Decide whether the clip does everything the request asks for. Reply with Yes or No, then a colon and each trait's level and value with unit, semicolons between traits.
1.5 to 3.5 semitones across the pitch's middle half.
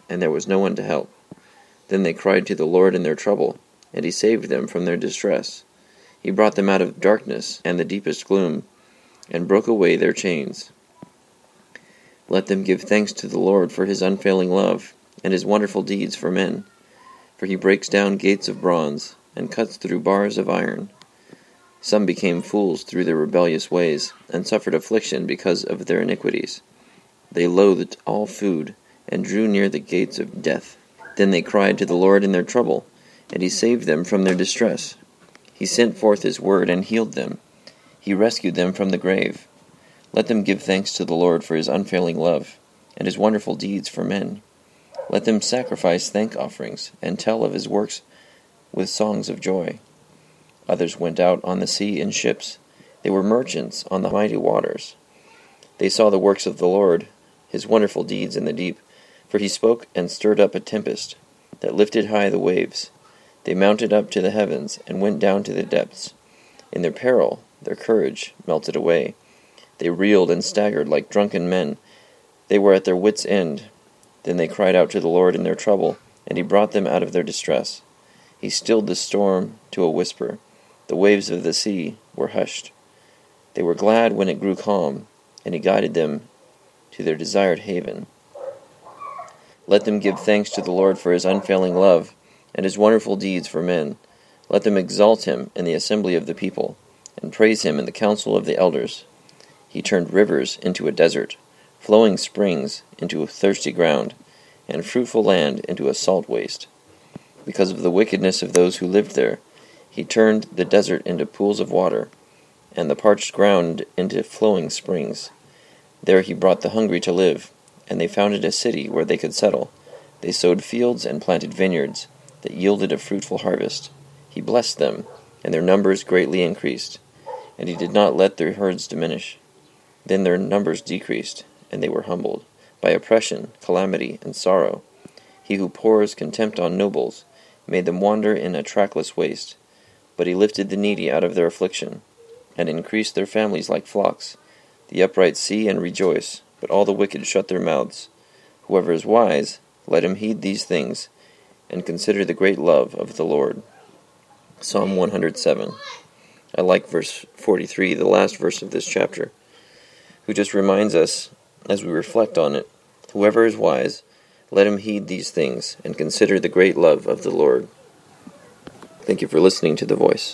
Yes: narrow, 2.4 semitones